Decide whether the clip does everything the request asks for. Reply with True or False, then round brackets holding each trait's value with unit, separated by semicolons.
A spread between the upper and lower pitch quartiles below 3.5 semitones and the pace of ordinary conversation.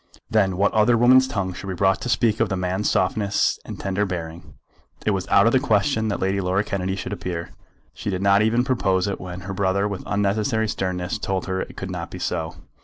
False (2.5 semitones; 225 wpm)